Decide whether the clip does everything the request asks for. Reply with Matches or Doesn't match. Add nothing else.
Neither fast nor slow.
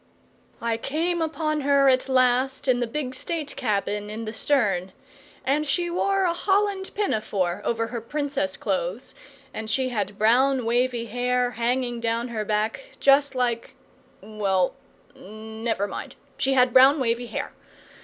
Matches